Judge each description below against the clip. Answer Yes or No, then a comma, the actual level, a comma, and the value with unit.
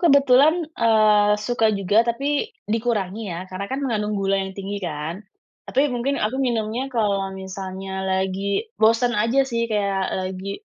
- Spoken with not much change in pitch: No, average, 3.8 semitones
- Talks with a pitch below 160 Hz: No, high, 210 Hz